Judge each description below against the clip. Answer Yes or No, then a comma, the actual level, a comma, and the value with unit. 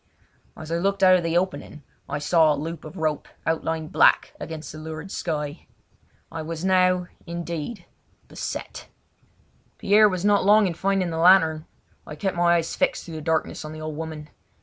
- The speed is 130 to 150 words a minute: No, average, 185 wpm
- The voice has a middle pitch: Yes, medium, 165 Hz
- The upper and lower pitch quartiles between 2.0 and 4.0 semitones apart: Yes, average, 2.8 semitones